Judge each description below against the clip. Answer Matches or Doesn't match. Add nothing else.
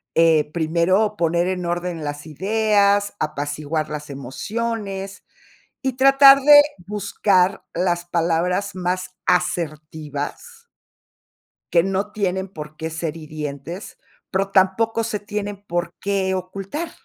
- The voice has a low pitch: Doesn't match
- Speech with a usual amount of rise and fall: Matches